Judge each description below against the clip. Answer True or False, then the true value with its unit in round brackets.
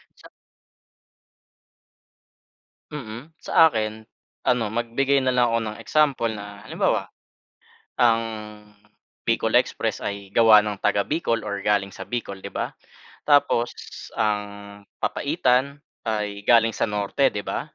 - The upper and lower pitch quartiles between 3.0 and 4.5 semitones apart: True (3.4 semitones)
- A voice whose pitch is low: True (115 Hz)